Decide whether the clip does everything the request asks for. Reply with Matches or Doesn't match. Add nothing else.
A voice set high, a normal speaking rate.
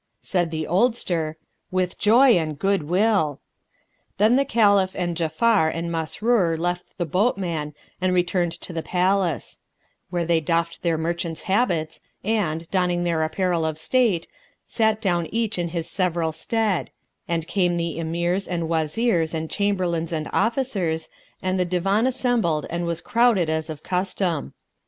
Doesn't match